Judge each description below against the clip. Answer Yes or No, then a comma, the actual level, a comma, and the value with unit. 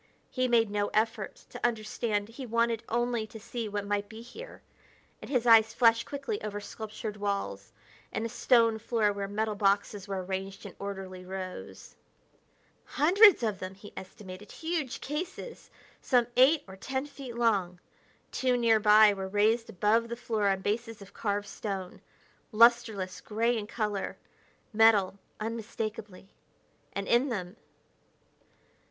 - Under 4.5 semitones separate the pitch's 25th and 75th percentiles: Yes, average, 2.8 semitones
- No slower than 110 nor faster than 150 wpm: Yes, average, 145 wpm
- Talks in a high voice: Yes, high, 220 Hz